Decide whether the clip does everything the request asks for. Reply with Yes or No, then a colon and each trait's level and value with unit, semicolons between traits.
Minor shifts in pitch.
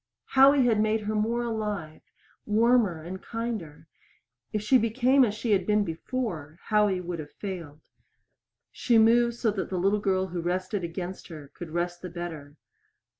No: average, 4.6 semitones